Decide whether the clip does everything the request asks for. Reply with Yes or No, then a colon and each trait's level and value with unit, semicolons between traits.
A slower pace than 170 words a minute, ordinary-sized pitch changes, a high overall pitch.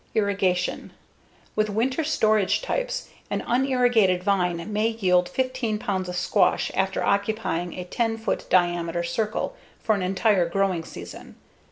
Yes: slow, 135 wpm; average, 3.8 semitones; high, 200 Hz